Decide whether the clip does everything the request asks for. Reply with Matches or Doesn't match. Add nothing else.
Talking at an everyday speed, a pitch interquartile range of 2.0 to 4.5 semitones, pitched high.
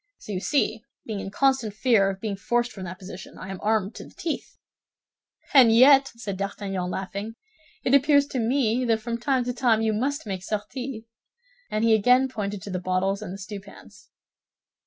Matches